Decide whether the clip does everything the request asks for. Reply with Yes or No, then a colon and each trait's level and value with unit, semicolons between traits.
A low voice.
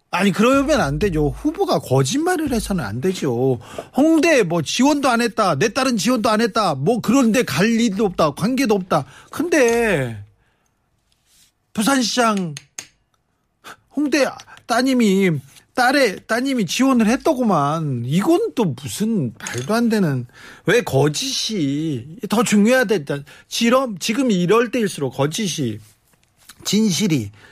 No: high, 215 Hz